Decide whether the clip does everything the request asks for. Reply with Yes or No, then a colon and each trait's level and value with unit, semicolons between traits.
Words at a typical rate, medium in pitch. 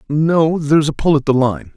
No: fast, 240 wpm; medium, 150 Hz